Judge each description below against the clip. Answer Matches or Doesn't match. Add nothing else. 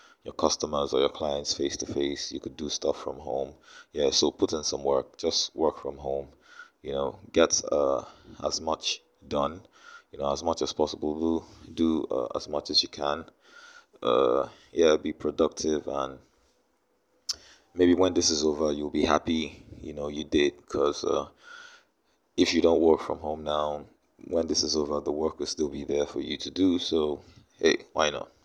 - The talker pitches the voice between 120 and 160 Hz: Doesn't match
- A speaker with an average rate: Matches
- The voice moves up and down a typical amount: Doesn't match